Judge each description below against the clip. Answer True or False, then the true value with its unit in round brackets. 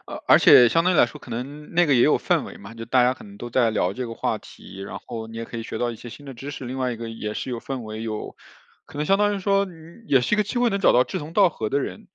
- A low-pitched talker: True (125 Hz)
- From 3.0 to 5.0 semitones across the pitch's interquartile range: True (4.7 semitones)